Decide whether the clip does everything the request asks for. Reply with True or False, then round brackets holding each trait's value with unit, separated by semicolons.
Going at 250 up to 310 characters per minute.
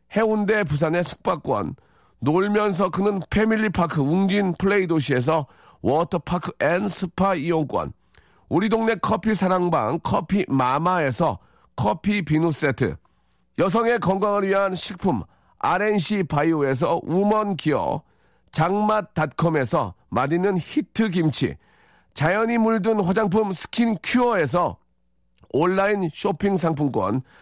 True (255 characters per minute)